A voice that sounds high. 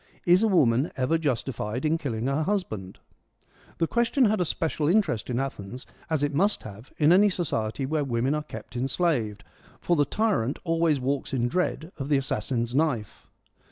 No: medium, 145 Hz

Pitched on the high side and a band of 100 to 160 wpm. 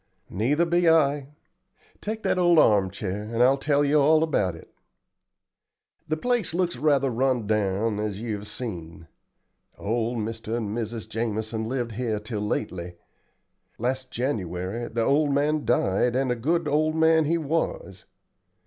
No: low, 120 Hz; average, 150 wpm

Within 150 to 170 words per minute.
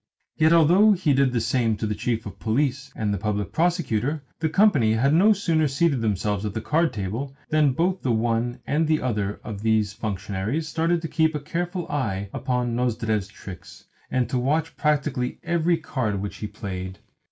No: average, 185 wpm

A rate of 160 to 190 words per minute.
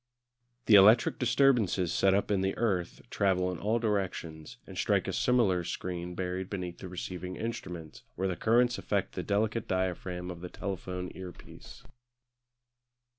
No: average, 150 wpm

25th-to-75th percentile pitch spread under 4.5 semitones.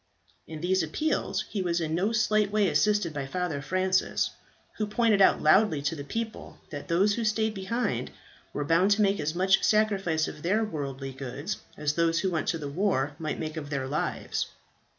No: average, 5.3 semitones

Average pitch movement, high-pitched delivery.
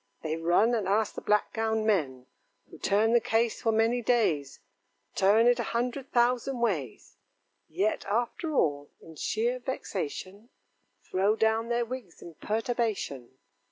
Yes: average, 4.3 semitones; high, 220 Hz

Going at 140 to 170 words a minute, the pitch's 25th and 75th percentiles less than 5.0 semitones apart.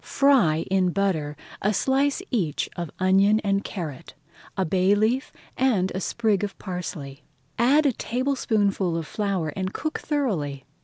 No: average, 145 wpm; average, 5.3 semitones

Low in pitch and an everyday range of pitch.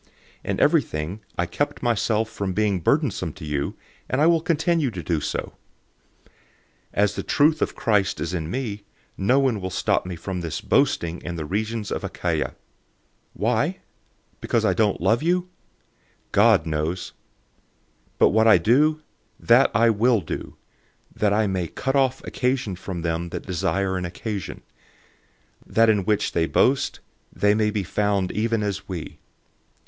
Yes: low, 105 Hz; average, 4.6 semitones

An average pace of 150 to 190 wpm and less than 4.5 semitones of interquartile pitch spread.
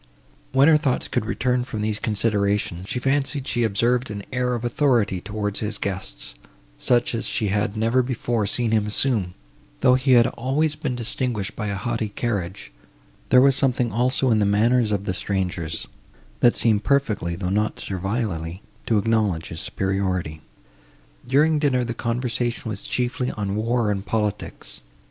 Yes: average, 165 wpm; average, 3.8 semitones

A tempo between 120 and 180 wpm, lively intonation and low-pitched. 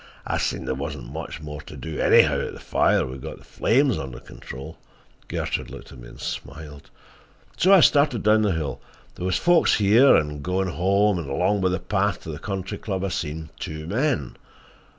No: average, 190 wpm; wide, 5.8 semitones; very low, 90 Hz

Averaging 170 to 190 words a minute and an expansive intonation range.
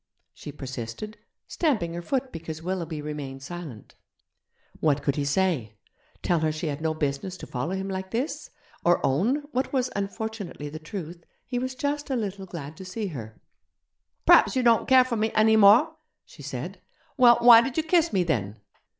Yes: average, 180 wpm; wide, 7.6 semitones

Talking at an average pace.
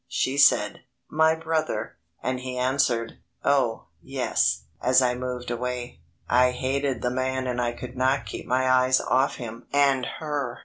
Yes: average, 160 wpm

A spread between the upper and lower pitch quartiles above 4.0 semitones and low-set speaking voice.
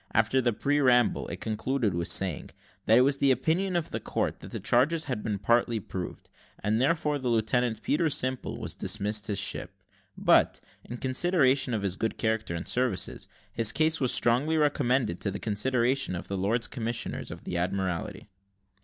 Yes: average, 4.5 semitones; low, 120 Hz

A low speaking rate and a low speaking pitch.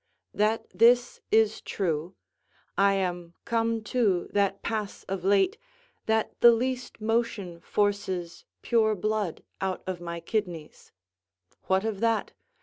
No: slow, 125 wpm; high, 205 Hz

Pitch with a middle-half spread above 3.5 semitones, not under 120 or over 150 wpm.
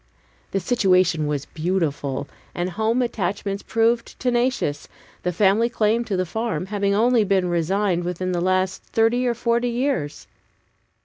Yes: average, 4.7 semitones; average, 140 wpm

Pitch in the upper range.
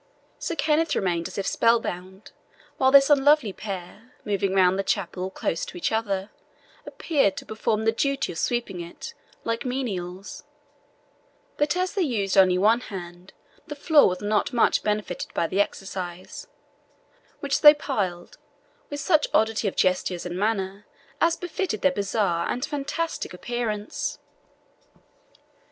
Yes: high, 210 Hz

